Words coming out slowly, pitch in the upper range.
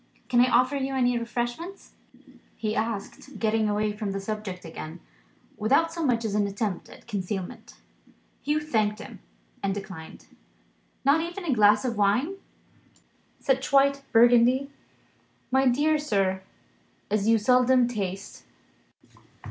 Yes: slow, 130 wpm; high, 230 Hz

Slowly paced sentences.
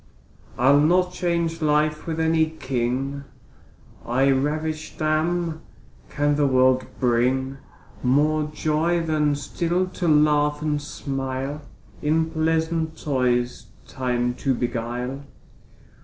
Yes: slow, 105 wpm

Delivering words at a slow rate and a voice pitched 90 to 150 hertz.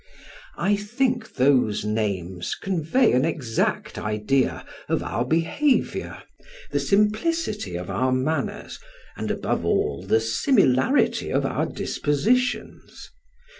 Yes: slow, 105 wpm; medium, 140 Hz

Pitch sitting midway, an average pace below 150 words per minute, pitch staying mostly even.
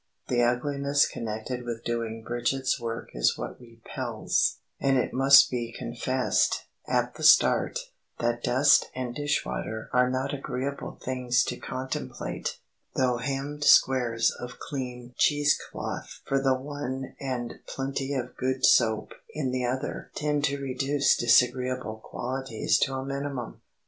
No: low, 130 Hz; average, 140 wpm; narrow, 2.2 semitones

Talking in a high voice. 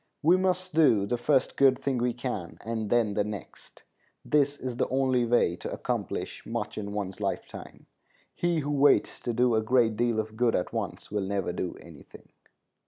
No: low, 120 Hz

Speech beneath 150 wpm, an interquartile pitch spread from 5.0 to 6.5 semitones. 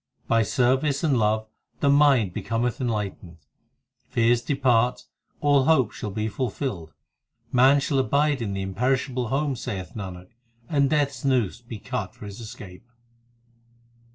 No: average, 140 wpm; average, 4.4 semitones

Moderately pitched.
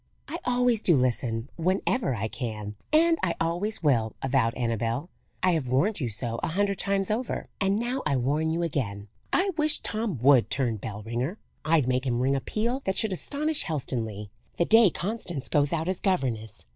Yes: medium, 155 Hz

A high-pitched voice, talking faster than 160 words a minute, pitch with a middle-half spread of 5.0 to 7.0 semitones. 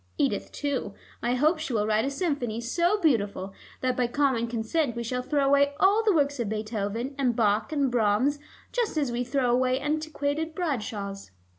No: very high, 255 Hz; average, 180 wpm; average, 4.3 semitones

